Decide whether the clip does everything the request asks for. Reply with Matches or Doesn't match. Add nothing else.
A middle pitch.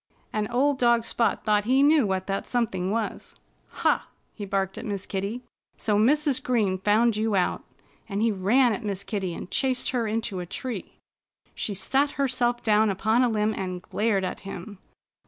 Doesn't match